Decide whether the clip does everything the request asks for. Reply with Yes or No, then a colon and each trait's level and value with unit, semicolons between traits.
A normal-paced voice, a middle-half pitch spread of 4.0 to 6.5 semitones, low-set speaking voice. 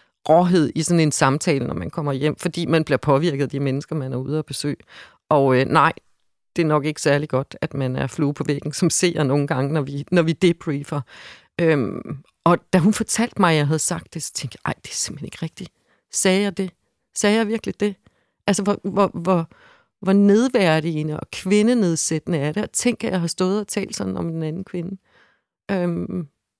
No: average, 215 wpm; average, 4.5 semitones; medium, 165 Hz